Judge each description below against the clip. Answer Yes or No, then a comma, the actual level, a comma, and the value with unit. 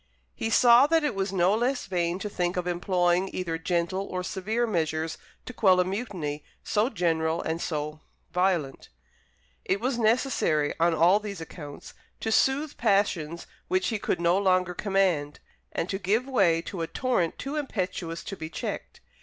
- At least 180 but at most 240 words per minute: No, average, 170 wpm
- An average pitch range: Yes, average, 4.2 semitones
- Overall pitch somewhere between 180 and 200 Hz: Yes, medium, 185 Hz